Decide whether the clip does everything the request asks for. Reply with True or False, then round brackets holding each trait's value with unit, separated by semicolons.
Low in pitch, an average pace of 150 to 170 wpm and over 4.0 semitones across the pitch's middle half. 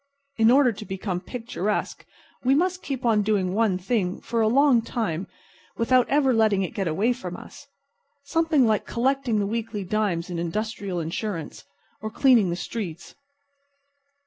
False (220 Hz; 155 wpm; 4.5 semitones)